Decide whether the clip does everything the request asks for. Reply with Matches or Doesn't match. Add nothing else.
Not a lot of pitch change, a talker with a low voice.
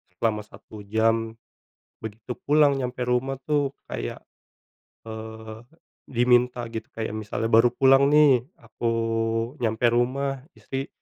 Doesn't match